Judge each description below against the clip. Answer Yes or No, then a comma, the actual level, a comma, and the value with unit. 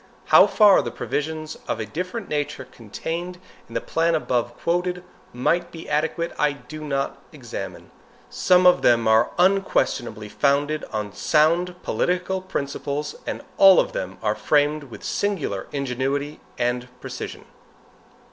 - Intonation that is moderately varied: No, wide, 5.9 semitones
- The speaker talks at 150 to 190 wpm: No, average, 140 wpm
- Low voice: No, medium, 150 Hz